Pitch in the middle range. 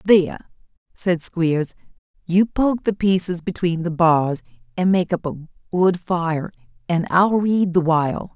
Yes: medium, 175 Hz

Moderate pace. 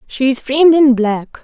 Yes: average, 165 wpm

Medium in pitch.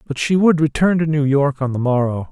Yes: medium, 145 Hz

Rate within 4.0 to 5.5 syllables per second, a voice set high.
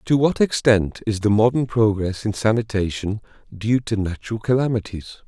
No: 5.1 syllables/s; low, 110 Hz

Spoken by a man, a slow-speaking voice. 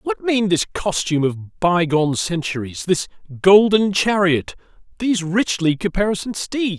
Yes: male; slow, 115 wpm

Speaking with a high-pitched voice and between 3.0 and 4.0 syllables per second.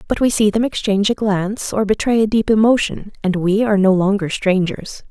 No: high, 205 Hz; 5.6 syllables/s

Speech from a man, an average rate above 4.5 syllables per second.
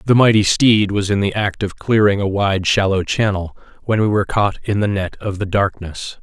Yes: male; 5.1 syllables/s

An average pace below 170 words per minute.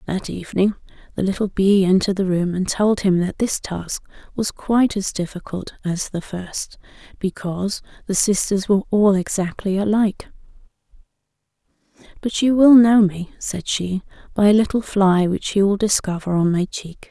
Yes: average, 160 wpm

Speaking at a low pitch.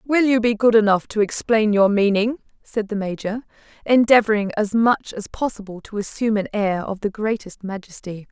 No: high, 215 Hz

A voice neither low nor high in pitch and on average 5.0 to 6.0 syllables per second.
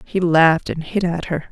Yes: medium, 170 Hz; 5.1 syllables/s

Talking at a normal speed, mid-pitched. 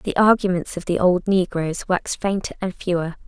Yes: average, 185 wpm; medium, 180 Hz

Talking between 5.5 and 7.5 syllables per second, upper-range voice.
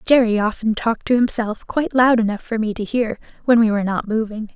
Yes: 6.0 syllables/s; high, 225 Hz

